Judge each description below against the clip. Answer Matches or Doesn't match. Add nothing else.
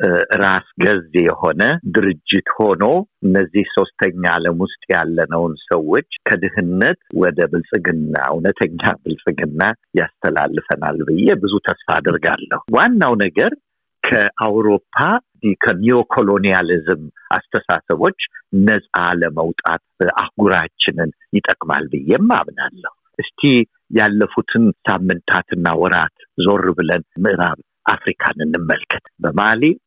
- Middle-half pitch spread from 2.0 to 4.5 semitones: Doesn't match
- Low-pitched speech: Matches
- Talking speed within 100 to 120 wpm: Doesn't match